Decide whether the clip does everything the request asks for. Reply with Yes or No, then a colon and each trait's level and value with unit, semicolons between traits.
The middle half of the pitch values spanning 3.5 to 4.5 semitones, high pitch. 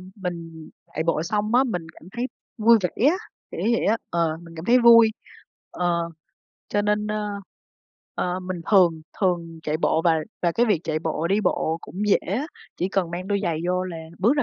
No: average, 4.1 semitones; medium, 180 Hz